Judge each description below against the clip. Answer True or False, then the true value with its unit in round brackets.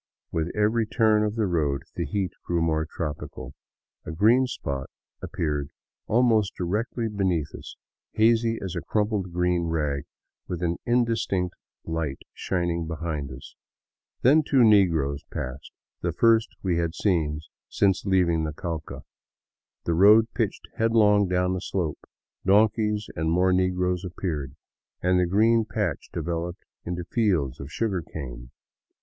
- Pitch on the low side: True (90 Hz)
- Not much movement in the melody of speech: False (4.7 semitones)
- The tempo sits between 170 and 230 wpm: False (135 wpm)